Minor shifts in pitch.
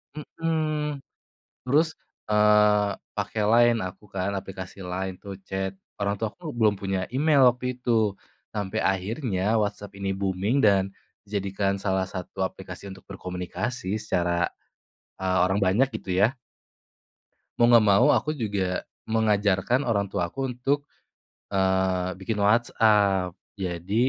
No: average, 3.6 semitones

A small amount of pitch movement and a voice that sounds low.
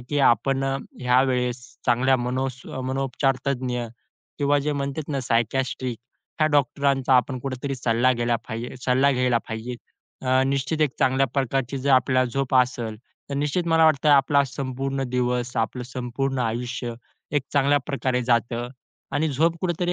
Yes: narrow, 1.9 semitones; low, 130 Hz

